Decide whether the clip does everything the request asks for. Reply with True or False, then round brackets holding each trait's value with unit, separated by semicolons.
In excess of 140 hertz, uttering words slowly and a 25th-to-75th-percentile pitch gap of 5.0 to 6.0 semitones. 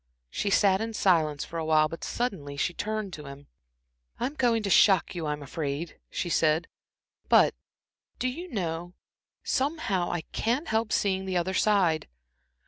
False (185 Hz; 155 wpm; 5.3 semitones)